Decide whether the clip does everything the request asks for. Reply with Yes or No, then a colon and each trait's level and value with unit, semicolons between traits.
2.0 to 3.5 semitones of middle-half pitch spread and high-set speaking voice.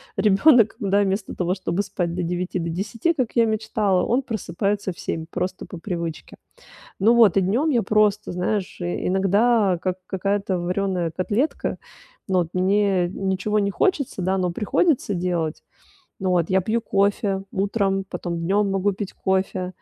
Yes: narrow, 2.5 semitones; high, 195 Hz